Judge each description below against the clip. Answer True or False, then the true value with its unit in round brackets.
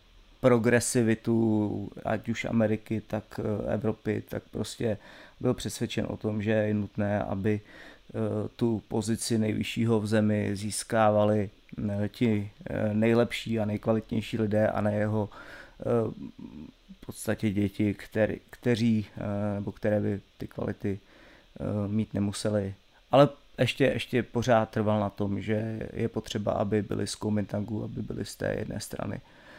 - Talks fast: False (125 wpm)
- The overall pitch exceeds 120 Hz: False (110 Hz)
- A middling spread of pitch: False (1.6 semitones)